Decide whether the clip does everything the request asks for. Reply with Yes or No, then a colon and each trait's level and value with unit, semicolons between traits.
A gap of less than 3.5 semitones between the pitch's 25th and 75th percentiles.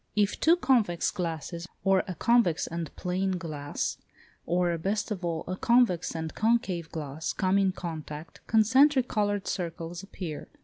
No: average, 4.0 semitones